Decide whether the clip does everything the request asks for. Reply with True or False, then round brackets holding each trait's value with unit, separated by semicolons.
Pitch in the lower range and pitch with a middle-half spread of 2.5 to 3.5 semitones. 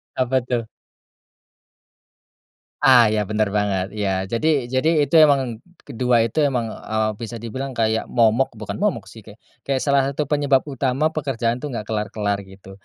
False (120 Hz; 3.9 semitones)